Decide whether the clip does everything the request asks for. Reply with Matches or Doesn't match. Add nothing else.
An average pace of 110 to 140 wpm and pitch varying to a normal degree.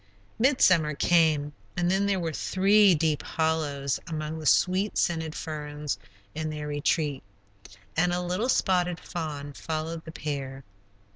Matches